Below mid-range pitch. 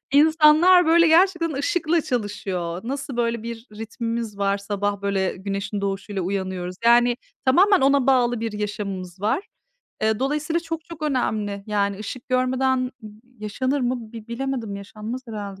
No: high, 235 Hz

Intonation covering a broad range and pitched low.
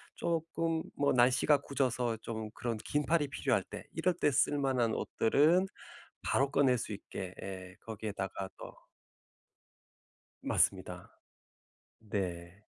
Yes: wide, 5.7 semitones; low, 125 Hz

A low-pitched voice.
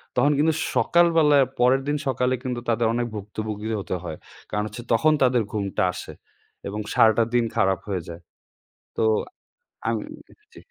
Yes: low, 115 Hz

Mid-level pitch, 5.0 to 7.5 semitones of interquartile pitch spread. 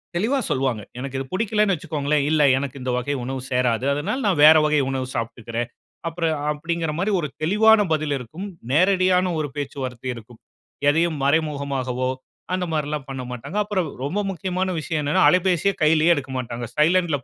Yes: medium, 150 Hz; average, 5.3 semitones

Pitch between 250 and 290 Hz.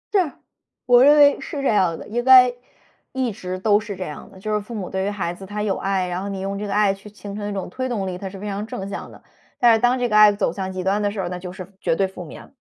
No: high, 200 Hz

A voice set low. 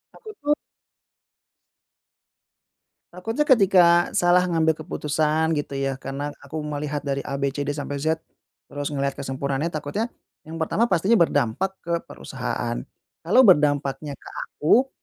No: medium, 155 Hz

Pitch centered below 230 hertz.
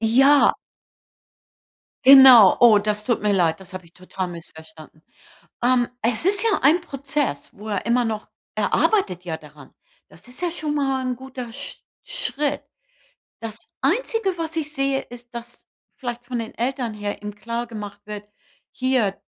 No: high, 240 Hz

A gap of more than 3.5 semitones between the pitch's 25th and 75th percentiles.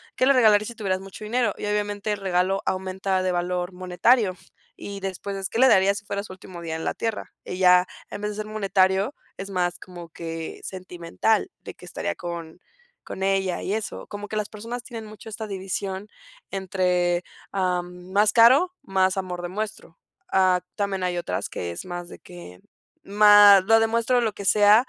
No: narrow, 2.6 semitones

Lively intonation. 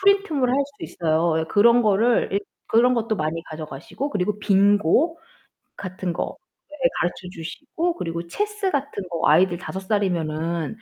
Yes: wide, 7.4 semitones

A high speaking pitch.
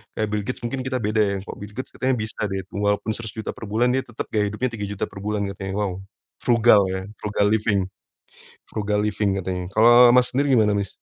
No: low, 105 Hz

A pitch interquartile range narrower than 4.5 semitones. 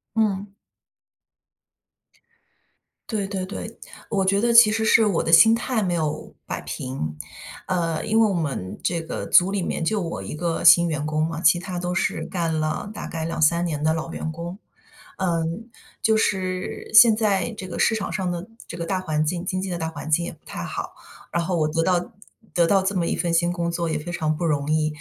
Yes: average, 3.2 semitones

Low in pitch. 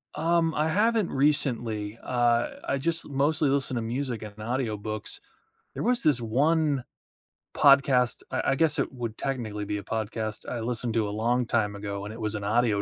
Yes: low, 120 Hz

